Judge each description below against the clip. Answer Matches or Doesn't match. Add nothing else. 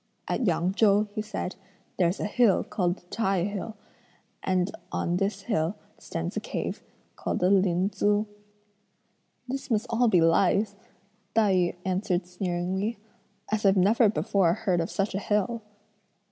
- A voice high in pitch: Matches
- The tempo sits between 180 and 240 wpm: Doesn't match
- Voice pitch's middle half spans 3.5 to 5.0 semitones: Doesn't match